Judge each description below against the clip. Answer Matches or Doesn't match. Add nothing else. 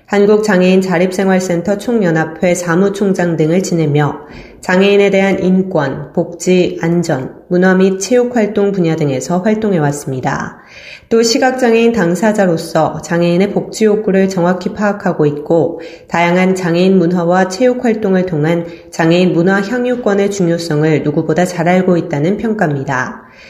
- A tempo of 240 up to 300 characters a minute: Doesn't match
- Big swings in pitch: Doesn't match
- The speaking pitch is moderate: Matches